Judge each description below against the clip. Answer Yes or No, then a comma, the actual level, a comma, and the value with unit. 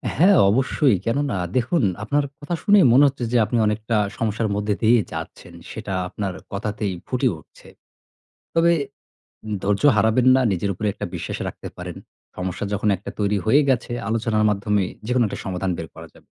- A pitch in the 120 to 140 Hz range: No, low, 110 Hz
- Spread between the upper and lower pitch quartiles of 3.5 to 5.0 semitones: Yes, average, 4.3 semitones